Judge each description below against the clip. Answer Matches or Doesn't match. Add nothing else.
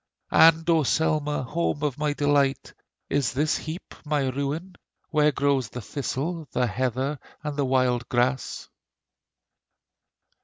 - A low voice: Doesn't match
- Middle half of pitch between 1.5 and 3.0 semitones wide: Matches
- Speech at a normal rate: Doesn't match